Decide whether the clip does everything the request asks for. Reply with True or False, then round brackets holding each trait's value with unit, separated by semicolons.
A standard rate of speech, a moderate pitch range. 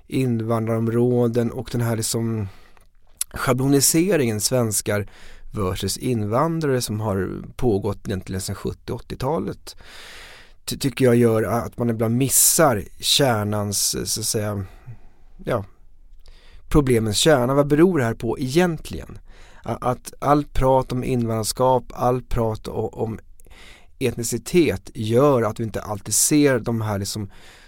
False (120 wpm; 4.1 semitones)